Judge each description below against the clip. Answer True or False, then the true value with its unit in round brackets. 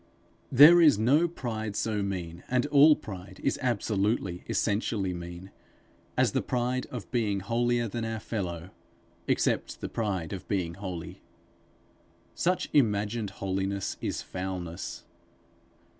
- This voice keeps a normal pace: False (125 wpm)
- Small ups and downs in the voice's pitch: False (4.3 semitones)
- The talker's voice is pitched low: True (105 Hz)